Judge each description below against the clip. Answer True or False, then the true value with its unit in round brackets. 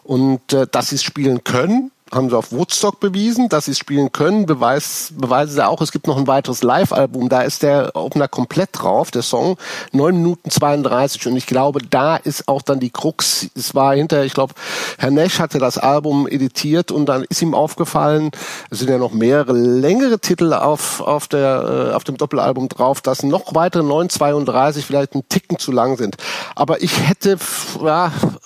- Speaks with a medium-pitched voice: True (145 Hz)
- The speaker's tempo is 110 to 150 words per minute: False (190 wpm)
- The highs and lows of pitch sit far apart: False (3.7 semitones)